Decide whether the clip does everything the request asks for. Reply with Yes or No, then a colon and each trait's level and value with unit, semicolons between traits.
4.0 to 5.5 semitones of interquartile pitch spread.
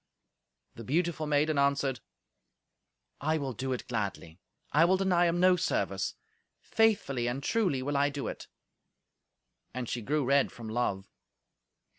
Yes: average, 5.2 semitones